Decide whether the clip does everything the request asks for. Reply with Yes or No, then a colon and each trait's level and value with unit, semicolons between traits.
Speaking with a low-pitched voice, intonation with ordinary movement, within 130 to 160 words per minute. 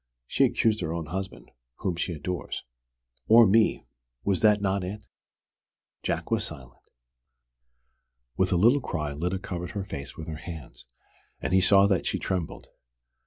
Yes: very low, 95 Hz; average, 3.5 semitones; average, 155 wpm